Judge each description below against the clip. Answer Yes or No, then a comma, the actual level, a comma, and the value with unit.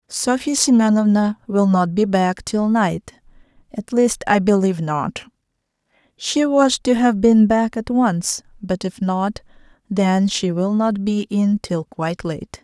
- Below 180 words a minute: Yes, average, 155 wpm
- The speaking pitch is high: Yes, high, 205 Hz